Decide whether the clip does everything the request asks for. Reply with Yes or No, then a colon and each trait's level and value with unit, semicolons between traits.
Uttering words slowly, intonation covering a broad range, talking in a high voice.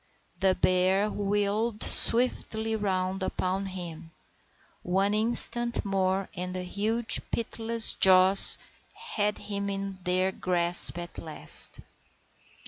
No: slow, 105 wpm; narrow, 2.4 semitones; high, 195 Hz